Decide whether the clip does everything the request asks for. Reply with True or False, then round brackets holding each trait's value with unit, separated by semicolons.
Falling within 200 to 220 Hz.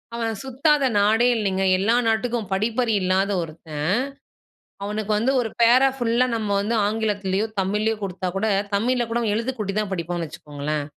True (215 Hz)